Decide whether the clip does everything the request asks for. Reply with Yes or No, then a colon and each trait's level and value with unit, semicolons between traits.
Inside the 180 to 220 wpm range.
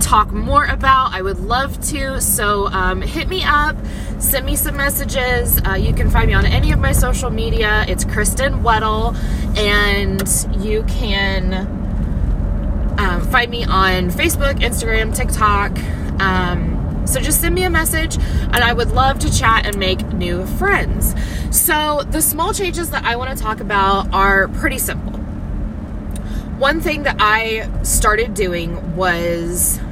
No: average, 155 wpm